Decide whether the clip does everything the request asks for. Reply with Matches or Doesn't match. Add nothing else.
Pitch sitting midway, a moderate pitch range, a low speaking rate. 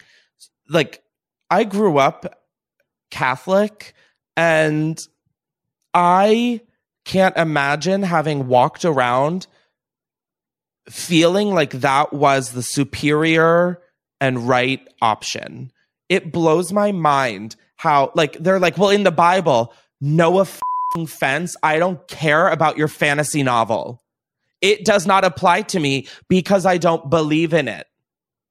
Matches